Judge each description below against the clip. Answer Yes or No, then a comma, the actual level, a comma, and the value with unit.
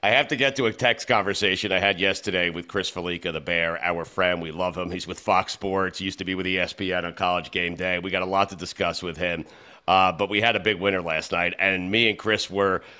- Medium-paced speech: No, fast, 265 wpm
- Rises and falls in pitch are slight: Yes, narrow, 2.0 semitones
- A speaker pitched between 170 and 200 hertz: No, very low, 95 Hz